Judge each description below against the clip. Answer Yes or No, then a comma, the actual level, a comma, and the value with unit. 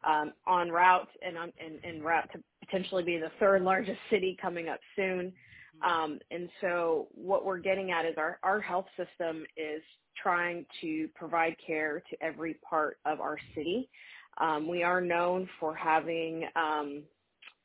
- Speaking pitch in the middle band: Yes, medium, 170 Hz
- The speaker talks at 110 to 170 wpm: Yes, average, 160 wpm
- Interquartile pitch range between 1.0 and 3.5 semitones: Yes, narrow, 2.5 semitones